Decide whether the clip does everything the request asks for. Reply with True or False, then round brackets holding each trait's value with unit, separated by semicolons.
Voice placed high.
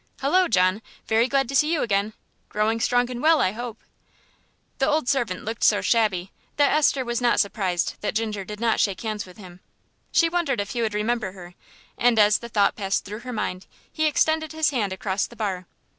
True (225 Hz)